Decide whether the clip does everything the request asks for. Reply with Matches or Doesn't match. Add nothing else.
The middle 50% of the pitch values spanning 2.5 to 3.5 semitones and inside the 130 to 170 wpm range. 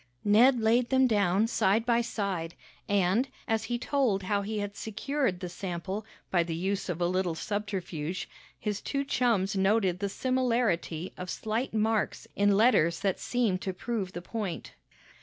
Doesn't match